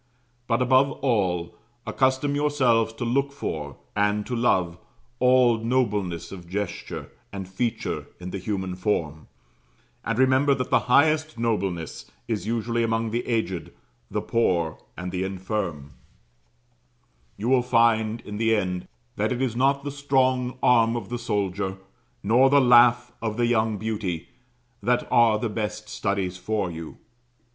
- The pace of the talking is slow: No, average, 145 wpm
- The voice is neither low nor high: No, low, 115 Hz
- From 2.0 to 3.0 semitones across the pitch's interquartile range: No, average, 4.4 semitones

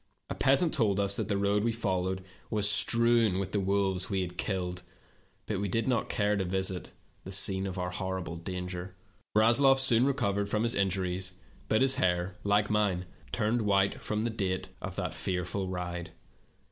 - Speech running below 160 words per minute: No, average, 180 wpm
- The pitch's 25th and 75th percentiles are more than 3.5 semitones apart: No, average, 2.8 semitones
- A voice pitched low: Yes, low, 100 Hz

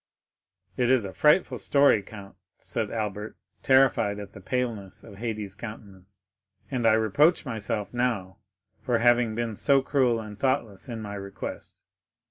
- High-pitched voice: No, low, 110 Hz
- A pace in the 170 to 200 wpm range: No, average, 145 wpm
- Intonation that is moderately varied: Yes, average, 3.7 semitones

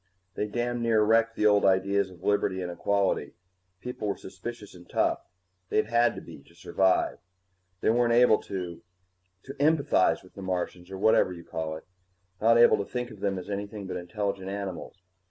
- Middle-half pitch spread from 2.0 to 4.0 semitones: Yes, average, 3.6 semitones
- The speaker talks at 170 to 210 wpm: Yes, average, 180 wpm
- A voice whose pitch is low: Yes, low, 100 Hz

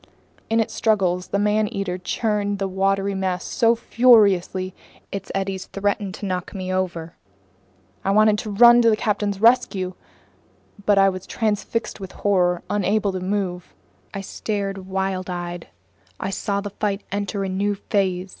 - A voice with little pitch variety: Yes, narrow, 1.9 semitones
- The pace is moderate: Yes, average, 155 wpm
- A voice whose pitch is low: No, high, 195 Hz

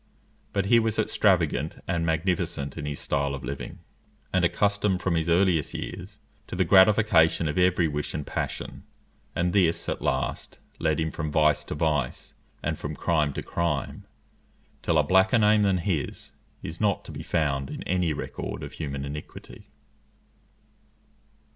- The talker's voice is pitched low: Yes, very low, 85 Hz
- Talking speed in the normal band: Yes, average, 160 wpm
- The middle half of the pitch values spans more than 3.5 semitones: Yes, average, 4.0 semitones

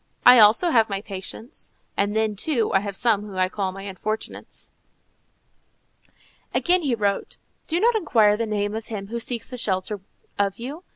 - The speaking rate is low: No, average, 175 wpm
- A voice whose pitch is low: No, high, 215 Hz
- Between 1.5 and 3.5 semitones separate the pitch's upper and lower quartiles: Yes, average, 3.1 semitones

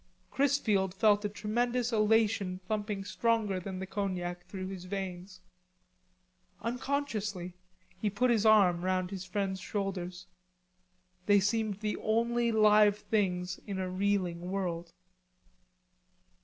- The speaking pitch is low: No, high, 200 Hz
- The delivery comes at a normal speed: No, slow, 115 wpm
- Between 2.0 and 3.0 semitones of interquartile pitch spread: Yes, average, 2.7 semitones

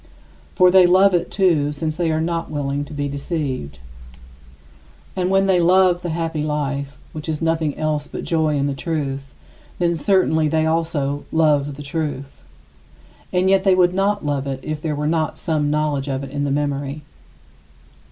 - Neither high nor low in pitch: Yes, medium, 155 Hz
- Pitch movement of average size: Yes, average, 3.1 semitones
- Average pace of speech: Yes, average, 180 wpm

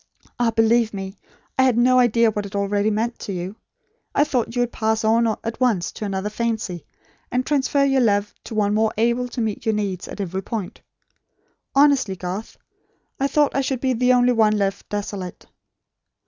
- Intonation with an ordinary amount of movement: Yes, average, 3.4 semitones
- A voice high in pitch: Yes, high, 220 Hz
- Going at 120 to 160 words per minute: No, average, 190 wpm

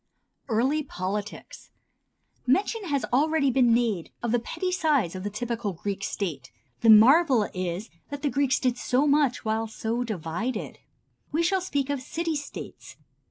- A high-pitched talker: Yes, high, 245 Hz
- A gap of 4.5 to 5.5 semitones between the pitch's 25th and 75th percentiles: Yes, average, 5.2 semitones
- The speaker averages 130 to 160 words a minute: Yes, average, 155 wpm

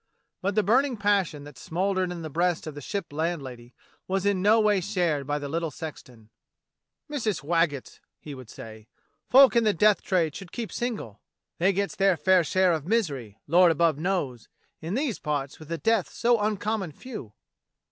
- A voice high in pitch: No, medium, 175 Hz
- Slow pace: No, average, 180 wpm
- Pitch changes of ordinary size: No, wide, 5.8 semitones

